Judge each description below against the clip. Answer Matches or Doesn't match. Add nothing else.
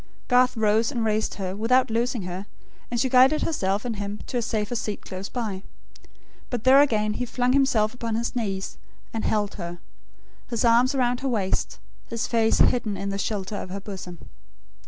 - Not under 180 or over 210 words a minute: Matches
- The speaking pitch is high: Matches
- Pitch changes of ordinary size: Matches